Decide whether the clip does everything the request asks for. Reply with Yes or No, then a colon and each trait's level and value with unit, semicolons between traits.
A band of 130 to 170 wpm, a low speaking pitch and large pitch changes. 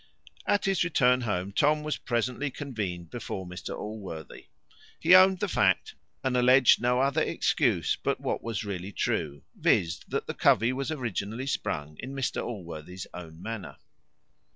Yes: average, 150 wpm; low, 115 Hz; wide, 6.8 semitones